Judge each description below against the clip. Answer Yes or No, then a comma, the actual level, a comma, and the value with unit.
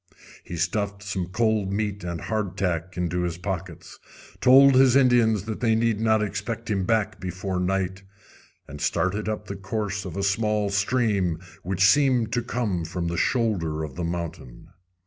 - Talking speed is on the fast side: No, average, 165 wpm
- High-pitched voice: No, low, 100 Hz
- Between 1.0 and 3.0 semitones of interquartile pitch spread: No, average, 3.5 semitones